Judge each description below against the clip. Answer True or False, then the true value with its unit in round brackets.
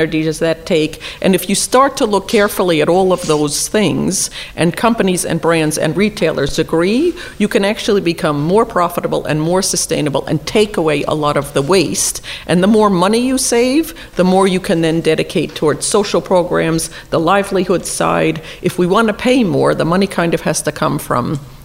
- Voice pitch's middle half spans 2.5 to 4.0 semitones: False (4.4 semitones)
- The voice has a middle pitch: True (180 Hz)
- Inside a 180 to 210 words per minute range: True (195 wpm)